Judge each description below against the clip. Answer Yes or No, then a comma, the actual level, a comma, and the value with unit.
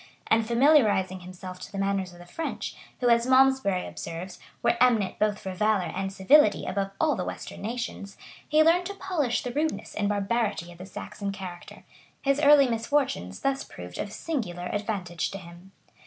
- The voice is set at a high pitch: Yes, high, 205 Hz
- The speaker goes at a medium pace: Yes, average, 175 wpm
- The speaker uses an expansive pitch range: Yes, wide, 5.9 semitones